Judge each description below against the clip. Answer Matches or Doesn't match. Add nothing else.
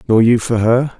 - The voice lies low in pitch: Matches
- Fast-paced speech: Matches